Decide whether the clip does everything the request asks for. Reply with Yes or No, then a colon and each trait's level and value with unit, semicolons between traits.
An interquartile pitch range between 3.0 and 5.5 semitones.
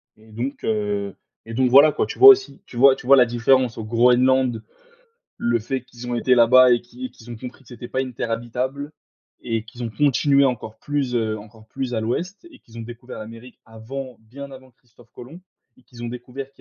No: narrow, 2.5 semitones